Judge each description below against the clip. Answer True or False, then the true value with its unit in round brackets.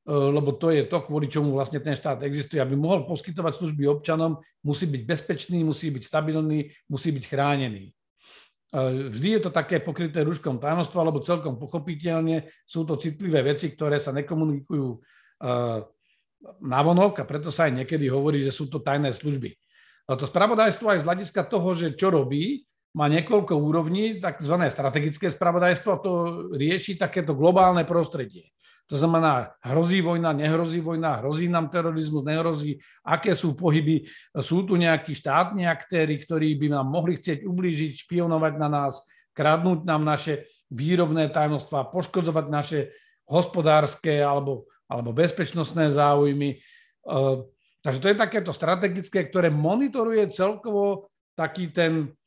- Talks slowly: False (140 wpm)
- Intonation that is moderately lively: True (3.1 semitones)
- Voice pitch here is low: False (160 Hz)